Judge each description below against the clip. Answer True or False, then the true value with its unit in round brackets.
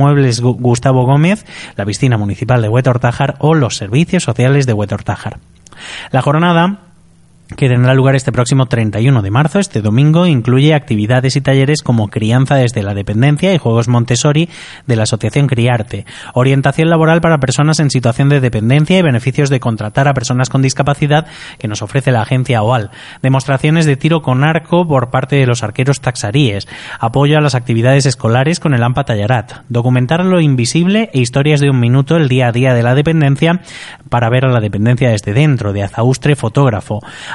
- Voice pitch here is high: False (130 Hz)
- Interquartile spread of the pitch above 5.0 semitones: False (3.5 semitones)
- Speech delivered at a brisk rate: False (175 wpm)